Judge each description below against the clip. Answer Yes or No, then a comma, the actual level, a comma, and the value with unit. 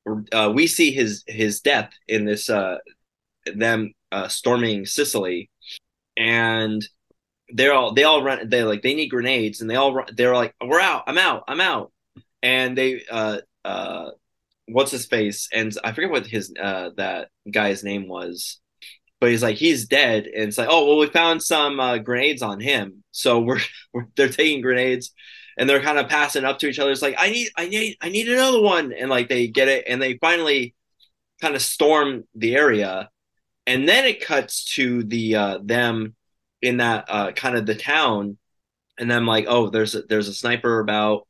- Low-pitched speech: Yes, low, 120 Hz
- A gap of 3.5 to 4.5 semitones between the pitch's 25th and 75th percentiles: Yes, average, 4.1 semitones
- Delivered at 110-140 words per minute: No, average, 195 wpm